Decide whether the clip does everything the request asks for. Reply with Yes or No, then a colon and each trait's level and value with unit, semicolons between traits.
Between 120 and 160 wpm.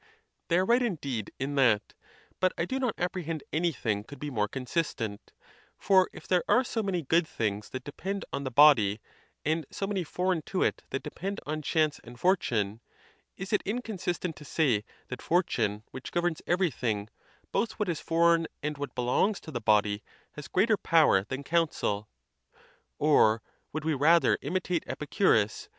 No: average, 175 wpm